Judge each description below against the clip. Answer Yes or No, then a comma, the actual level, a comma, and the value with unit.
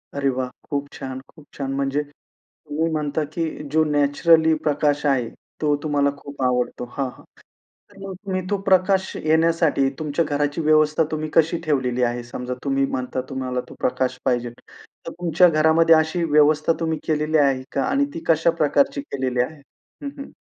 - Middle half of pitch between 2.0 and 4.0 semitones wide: Yes, average, 3.0 semitones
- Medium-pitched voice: Yes, medium, 150 Hz